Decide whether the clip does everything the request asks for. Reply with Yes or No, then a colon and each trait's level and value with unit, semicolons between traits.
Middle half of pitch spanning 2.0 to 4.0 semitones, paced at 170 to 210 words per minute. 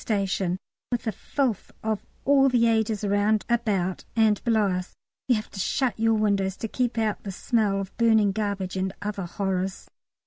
Yes: average, 2.7 semitones; average, 175 wpm